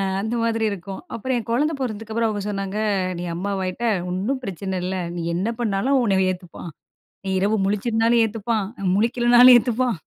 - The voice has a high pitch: Yes, high, 215 Hz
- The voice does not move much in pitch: No, average, 3.4 semitones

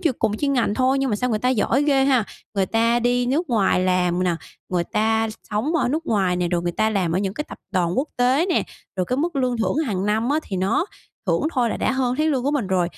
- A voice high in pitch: Yes, high, 230 Hz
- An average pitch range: No, wide, 5.8 semitones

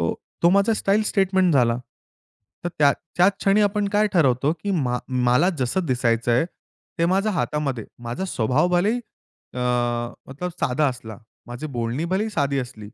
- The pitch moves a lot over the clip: Yes, wide, 7.5 semitones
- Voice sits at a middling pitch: Yes, medium, 155 Hz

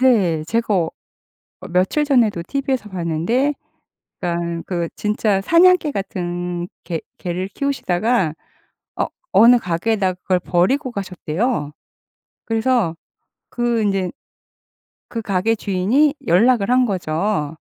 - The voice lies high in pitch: Yes, high, 200 Hz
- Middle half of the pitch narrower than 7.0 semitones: Yes, wide, 5.4 semitones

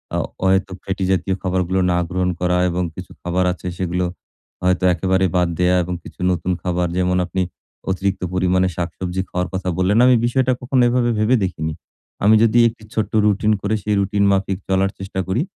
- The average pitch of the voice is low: Yes, very low, 95 Hz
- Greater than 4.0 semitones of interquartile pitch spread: No, narrow, 1.9 semitones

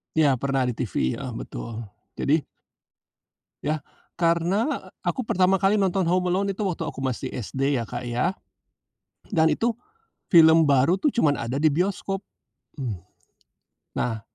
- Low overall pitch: No, medium, 160 Hz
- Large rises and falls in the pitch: Yes, wide, 6.1 semitones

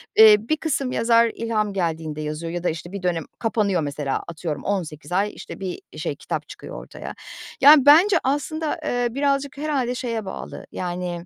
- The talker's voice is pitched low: No, high, 210 Hz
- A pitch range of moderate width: No, wide, 7.5 semitones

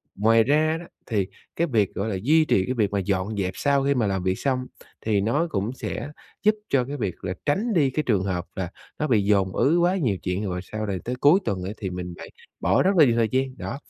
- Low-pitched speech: Yes, low, 115 Hz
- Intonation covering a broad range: Yes, wide, 6.6 semitones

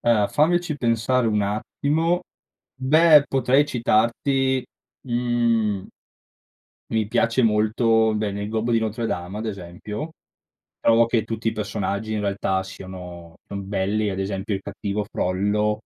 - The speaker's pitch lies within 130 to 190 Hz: No, low, 110 Hz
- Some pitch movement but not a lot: Yes, average, 3.0 semitones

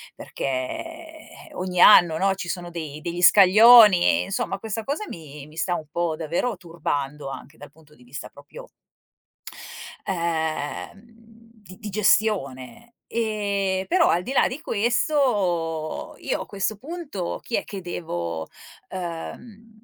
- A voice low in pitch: No, medium, 185 Hz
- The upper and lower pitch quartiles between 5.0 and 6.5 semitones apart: Yes, wide, 5.6 semitones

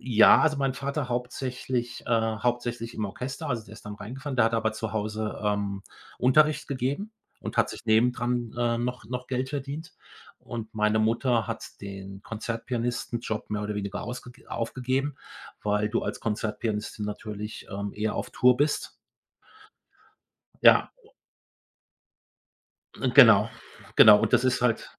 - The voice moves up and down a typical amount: Yes, average, 3.0 semitones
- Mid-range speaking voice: No, low, 120 Hz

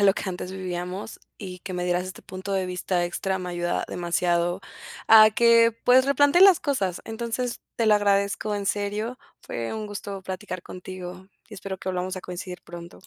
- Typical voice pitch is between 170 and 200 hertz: Yes, high, 190 Hz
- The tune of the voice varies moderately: Yes, average, 3.1 semitones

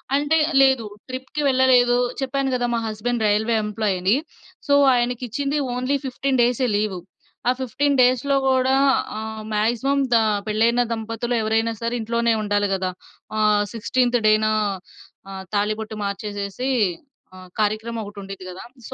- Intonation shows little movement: No, average, 3.3 semitones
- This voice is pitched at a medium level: No, high, 230 Hz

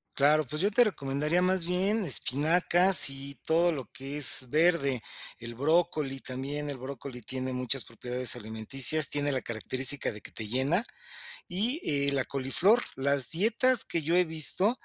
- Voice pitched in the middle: Yes, medium, 145 Hz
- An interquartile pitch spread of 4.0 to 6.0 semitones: Yes, average, 4.9 semitones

